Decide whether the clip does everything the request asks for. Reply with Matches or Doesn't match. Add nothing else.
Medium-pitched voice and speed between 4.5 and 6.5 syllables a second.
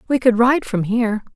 Doesn't match